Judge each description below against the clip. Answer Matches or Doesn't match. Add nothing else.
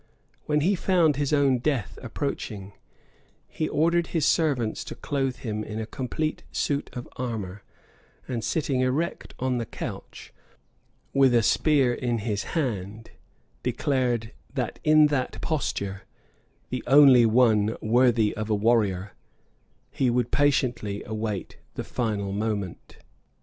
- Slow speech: Matches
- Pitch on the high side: Doesn't match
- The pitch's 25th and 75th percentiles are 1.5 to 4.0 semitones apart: Doesn't match